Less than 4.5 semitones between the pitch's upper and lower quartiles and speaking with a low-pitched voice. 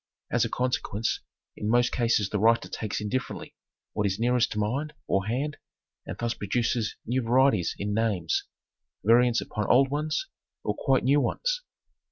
Yes: average, 3.5 semitones; low, 115 Hz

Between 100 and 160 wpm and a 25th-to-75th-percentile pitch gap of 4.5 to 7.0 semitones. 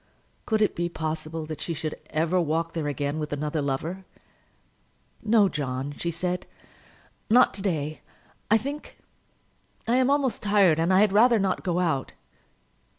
Yes: average, 155 wpm; average, 4.9 semitones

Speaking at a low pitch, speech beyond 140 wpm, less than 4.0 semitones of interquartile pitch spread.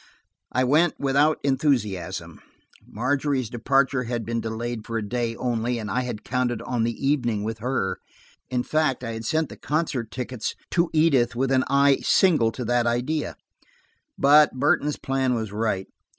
Yes: low, 125 Hz; average, 165 wpm; average, 3.3 semitones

